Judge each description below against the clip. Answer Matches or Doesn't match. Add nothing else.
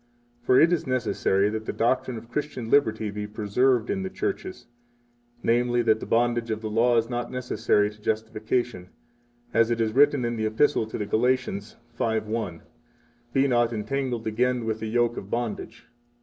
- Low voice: Matches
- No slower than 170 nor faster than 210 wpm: Matches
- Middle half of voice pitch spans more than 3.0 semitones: Doesn't match